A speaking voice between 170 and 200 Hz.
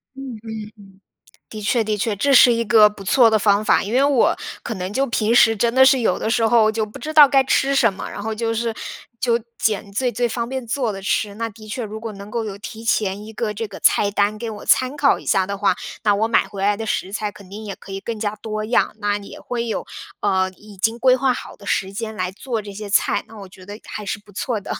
No: high, 220 Hz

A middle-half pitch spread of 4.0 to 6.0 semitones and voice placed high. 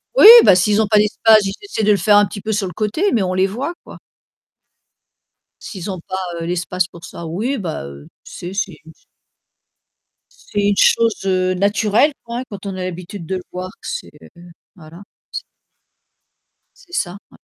No: average, 2.9 semitones; high, 195 Hz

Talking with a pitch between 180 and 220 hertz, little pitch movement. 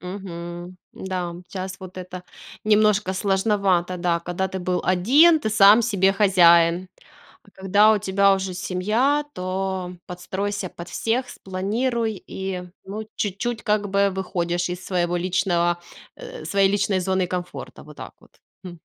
Yes: high, 190 Hz; narrow, 2.3 semitones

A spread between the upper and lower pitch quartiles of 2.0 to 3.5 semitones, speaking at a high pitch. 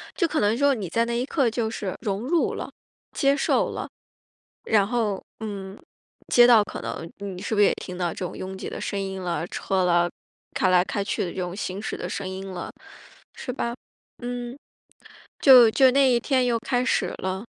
No: average, 4.4 semitones; high, 210 Hz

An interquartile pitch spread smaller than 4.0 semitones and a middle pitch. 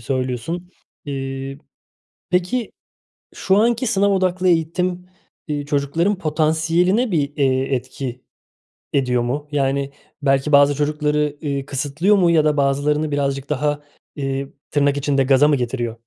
Yes: average, 3.6 semitones; medium, 145 Hz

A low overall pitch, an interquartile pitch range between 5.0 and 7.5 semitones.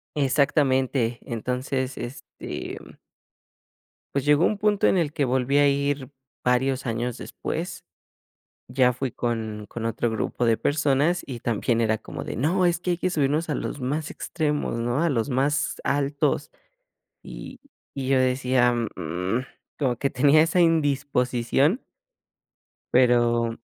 No: low, 130 Hz; average, 3.3 semitones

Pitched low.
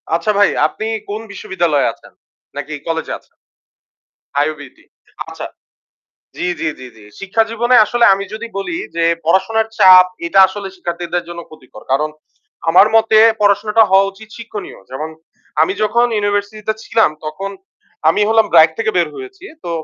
No: high, 195 Hz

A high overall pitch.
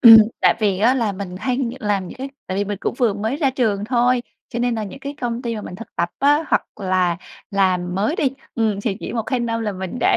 Yes: high, 220 Hz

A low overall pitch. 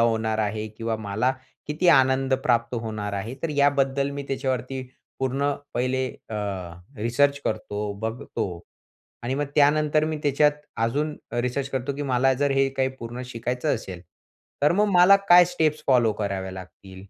Yes: low, 130 Hz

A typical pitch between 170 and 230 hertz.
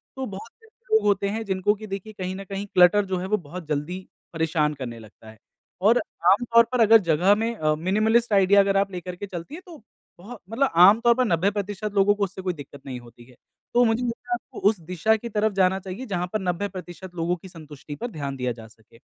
Yes: high, 190 Hz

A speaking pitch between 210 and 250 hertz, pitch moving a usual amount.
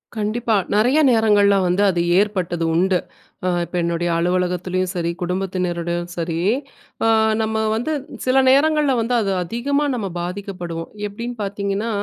No: high, 195 Hz; average, 4.2 semitones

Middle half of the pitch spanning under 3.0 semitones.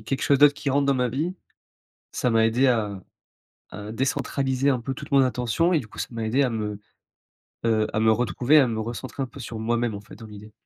No: average, 3.6 semitones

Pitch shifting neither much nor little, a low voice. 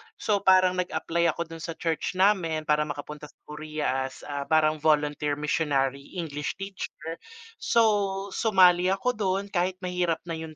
No: average, 3.8 semitones; medium, 165 Hz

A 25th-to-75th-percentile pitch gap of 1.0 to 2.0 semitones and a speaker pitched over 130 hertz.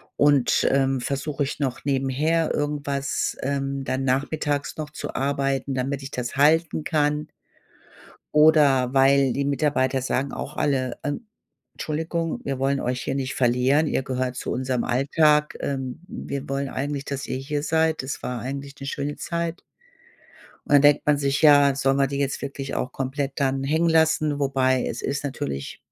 Yes: narrow, 1.7 semitones; medium, 140 Hz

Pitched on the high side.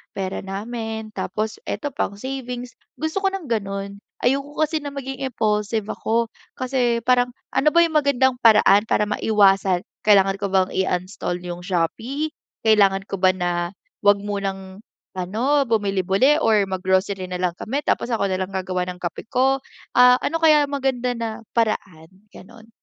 Yes: high, 215 Hz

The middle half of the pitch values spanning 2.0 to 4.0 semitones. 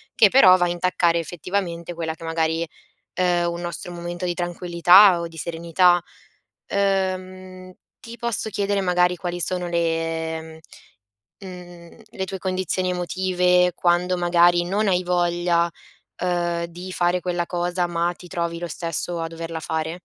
No: narrow, 1.2 semitones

